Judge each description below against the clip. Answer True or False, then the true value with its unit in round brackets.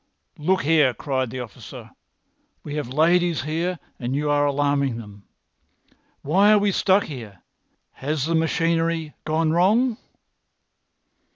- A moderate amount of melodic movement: True (3.7 semitones)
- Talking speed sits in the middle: False (125 wpm)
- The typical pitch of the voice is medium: True (155 Hz)